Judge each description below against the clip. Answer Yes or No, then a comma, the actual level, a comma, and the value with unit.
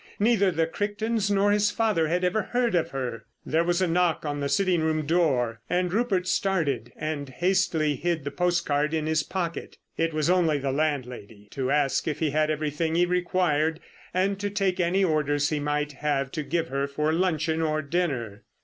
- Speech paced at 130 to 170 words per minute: No, average, 190 wpm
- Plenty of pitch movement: No, average, 3.7 semitones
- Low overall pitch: No, medium, 160 Hz